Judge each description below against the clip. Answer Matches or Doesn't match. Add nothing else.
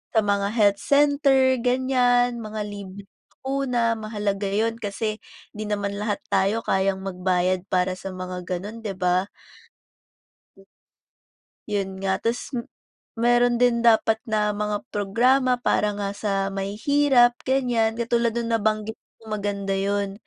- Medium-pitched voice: Doesn't match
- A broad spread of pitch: Doesn't match